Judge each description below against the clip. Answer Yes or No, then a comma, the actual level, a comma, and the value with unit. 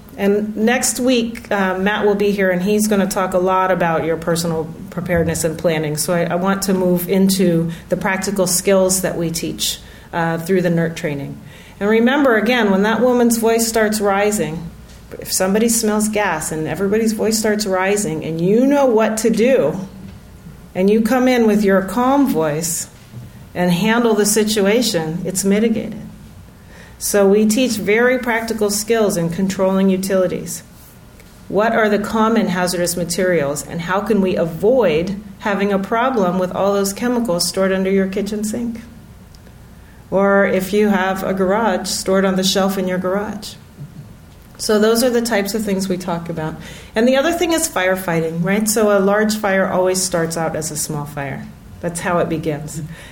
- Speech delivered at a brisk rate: No, average, 175 wpm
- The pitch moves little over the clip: No, average, 3.5 semitones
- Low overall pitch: No, high, 195 Hz